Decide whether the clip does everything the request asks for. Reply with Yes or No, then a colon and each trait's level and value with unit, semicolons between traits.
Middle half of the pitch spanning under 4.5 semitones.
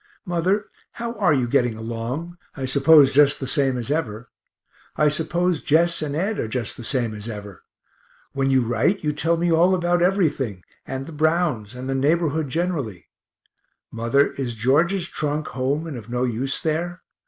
No: wide, 5.4 semitones